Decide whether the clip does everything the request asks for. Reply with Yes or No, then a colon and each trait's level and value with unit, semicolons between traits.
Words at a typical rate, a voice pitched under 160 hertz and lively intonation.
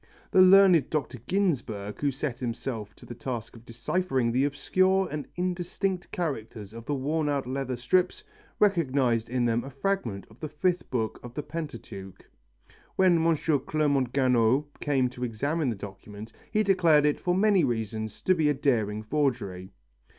Yes: average, 165 wpm; medium, 140 Hz; wide, 6.2 semitones